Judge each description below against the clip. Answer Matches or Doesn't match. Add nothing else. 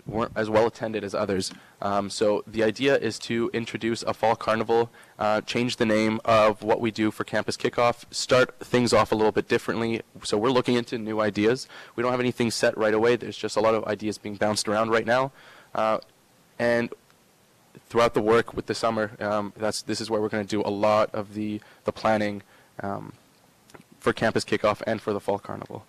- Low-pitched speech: Matches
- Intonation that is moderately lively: Doesn't match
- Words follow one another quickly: Matches